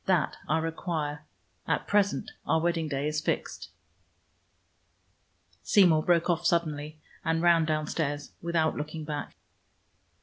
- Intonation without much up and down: Yes, narrow, 1.9 semitones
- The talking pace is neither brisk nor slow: No, slow, 115 wpm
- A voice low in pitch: No, medium, 160 Hz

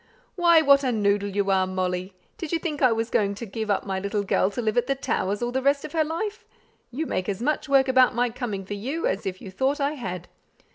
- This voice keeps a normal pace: No, fast, 255 wpm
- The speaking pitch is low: No, high, 230 Hz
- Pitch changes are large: Yes, wide, 5.9 semitones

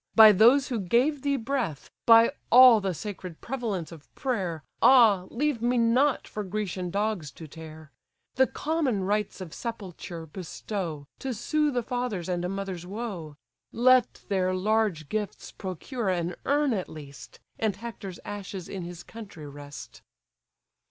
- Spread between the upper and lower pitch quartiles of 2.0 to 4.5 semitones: No, average, 5.2 semitones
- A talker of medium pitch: No, high, 205 Hz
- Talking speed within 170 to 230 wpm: No, average, 150 wpm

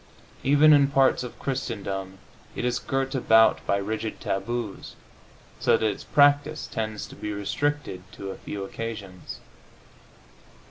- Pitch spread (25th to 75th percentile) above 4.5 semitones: Yes, average, 5.3 semitones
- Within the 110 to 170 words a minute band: Yes, slow, 135 wpm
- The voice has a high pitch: No, low, 115 Hz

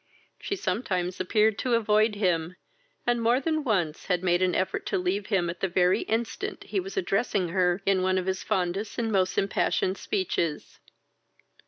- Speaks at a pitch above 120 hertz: Yes, high, 190 Hz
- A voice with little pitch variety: No, average, 3.5 semitones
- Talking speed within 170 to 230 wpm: Yes, average, 175 wpm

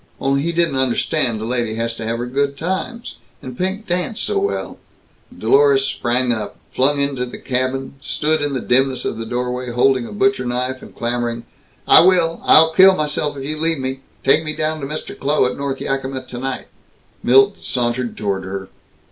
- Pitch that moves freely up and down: No, average, 4.1 semitones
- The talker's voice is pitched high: No, low, 135 Hz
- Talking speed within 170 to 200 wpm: Yes, average, 190 wpm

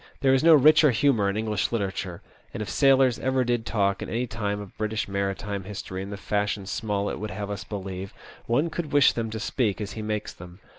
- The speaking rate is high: Yes, fast, 215 wpm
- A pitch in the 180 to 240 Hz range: No, low, 105 Hz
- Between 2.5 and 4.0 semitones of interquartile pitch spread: Yes, average, 3.4 semitones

